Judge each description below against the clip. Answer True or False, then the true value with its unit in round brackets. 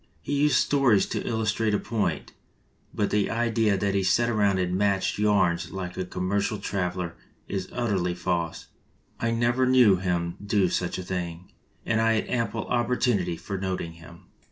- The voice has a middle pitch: False (100 Hz)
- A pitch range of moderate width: True (3.9 semitones)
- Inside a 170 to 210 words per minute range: True (175 wpm)